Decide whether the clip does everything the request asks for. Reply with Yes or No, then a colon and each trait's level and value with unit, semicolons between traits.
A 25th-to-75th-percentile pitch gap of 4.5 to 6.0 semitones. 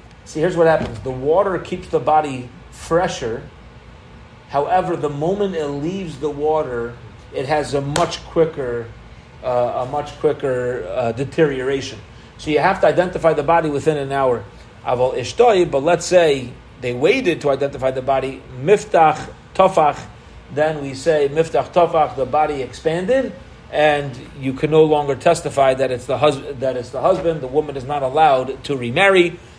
No: average, 3.7 semitones